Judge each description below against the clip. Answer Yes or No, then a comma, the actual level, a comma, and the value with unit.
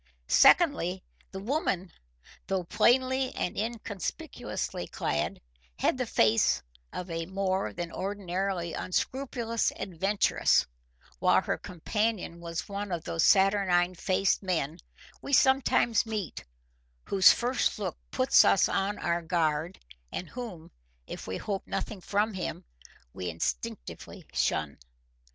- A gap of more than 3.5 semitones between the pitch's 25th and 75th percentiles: Yes, average, 4.1 semitones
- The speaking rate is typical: No, slow, 120 wpm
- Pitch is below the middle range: No, high, 190 Hz